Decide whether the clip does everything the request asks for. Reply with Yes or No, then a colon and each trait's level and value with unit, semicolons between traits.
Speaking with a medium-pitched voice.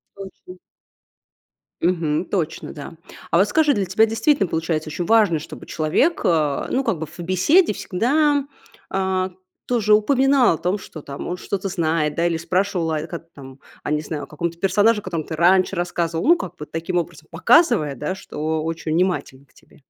Yes: medium, 175 Hz